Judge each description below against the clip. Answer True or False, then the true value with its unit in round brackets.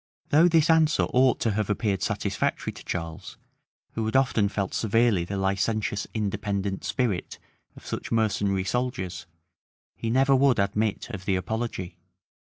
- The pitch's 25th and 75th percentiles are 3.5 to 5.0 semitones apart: True (4.0 semitones)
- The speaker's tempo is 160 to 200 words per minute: False (150 wpm)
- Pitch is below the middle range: True (105 Hz)